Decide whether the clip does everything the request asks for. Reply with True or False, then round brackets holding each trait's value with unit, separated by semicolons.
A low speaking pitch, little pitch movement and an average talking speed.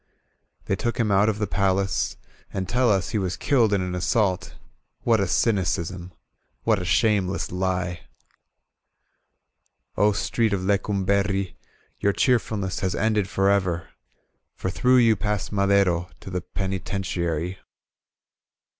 False (100 Hz; 2.3 semitones; 130 wpm)